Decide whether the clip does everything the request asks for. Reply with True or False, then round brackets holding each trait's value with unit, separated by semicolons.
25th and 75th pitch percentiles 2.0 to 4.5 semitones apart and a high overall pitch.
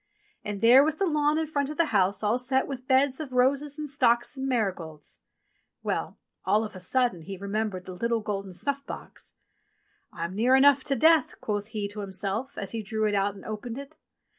False (5.4 semitones; 230 Hz)